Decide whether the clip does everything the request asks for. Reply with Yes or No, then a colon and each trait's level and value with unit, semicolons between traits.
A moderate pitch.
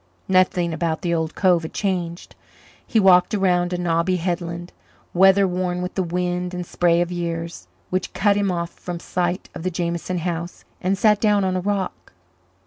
Yes: medium, 180 Hz